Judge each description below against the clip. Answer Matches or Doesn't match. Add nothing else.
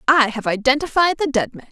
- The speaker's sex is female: Matches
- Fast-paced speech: Matches